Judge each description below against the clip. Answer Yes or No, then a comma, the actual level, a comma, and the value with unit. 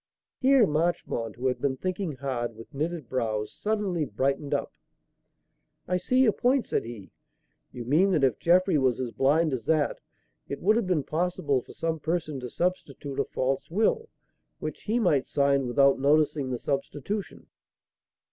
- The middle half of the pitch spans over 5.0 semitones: Yes, wide, 5.5 semitones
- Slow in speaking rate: No, average, 165 wpm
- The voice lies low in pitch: No, medium, 145 Hz